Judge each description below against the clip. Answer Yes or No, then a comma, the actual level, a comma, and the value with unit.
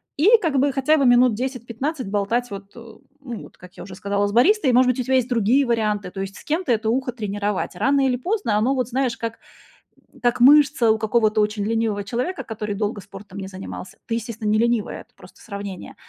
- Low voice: No, high, 230 Hz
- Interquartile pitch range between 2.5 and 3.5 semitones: No, average, 3.9 semitones